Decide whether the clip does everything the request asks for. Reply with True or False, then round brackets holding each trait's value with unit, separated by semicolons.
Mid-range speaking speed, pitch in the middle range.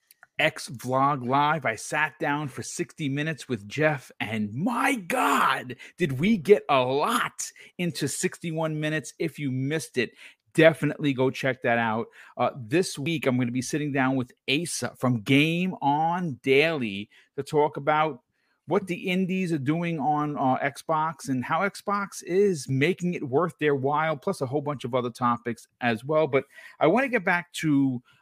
True (175 wpm; 150 Hz)